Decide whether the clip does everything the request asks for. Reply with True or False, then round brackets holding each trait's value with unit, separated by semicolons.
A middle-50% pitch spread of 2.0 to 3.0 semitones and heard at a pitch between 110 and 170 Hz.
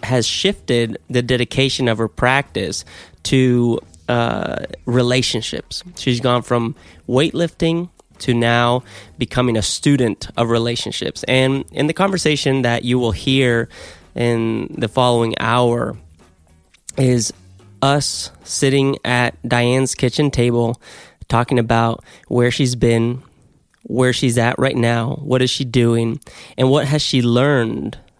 True (2.4 semitones; 120 Hz)